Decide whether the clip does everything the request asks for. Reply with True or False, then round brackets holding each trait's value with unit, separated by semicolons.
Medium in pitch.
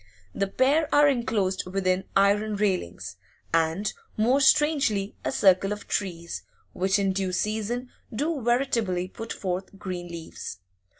False (200 Hz)